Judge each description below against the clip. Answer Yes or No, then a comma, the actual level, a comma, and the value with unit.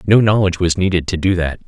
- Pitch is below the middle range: Yes, very low, 90 Hz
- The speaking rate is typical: No, fast, 250 wpm